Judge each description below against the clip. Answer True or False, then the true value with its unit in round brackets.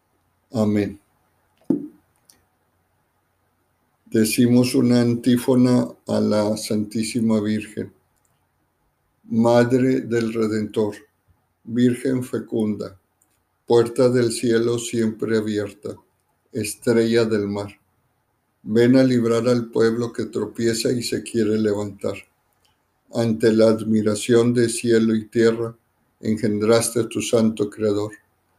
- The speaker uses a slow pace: True (90 wpm)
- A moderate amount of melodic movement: False (2.0 semitones)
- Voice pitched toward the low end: True (115 Hz)